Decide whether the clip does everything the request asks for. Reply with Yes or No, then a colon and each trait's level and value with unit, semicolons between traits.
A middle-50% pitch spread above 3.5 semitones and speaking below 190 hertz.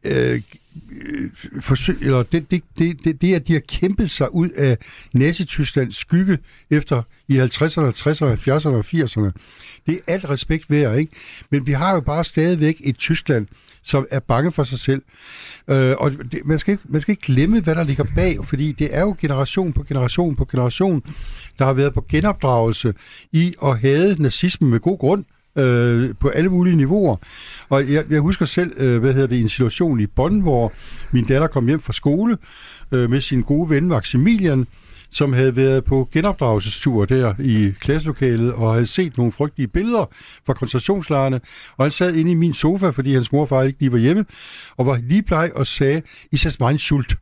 Yes: average, 4.1 semitones; medium, 140 Hz